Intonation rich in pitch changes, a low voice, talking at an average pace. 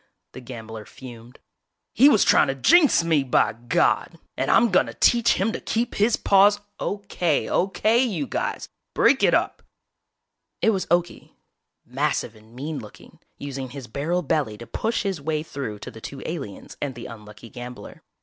No: wide, 8.3 semitones; medium, 145 Hz; average, 170 wpm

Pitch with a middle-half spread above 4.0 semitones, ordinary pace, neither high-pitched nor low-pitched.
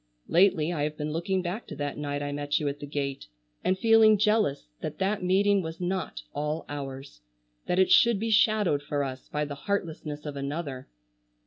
Yes: average, 5.0 semitones; average, 195 wpm; medium, 155 Hz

